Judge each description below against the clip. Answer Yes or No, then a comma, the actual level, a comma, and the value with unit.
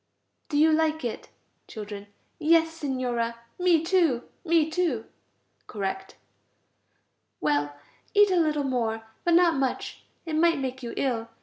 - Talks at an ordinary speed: No, slow, 130 wpm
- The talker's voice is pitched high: Yes, very high, 290 Hz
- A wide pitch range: Yes, wide, 5.9 semitones